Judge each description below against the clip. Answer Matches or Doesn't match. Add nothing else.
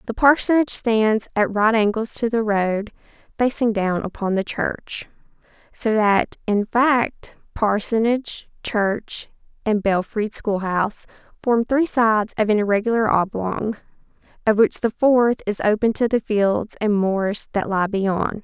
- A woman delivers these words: Matches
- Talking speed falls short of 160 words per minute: Matches